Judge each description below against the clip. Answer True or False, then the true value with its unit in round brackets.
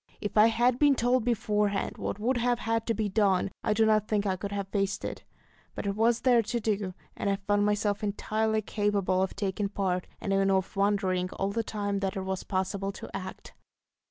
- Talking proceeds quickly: True (215 wpm)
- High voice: True (205 Hz)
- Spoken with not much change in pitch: True (2.1 semitones)